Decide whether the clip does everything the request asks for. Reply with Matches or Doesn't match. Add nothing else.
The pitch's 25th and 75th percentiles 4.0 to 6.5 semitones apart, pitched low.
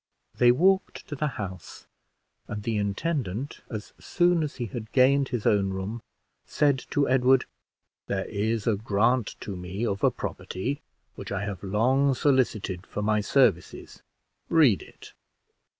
Matches